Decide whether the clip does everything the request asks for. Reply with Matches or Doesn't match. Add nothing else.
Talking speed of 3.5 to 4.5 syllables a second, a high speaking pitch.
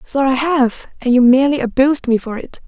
Doesn't match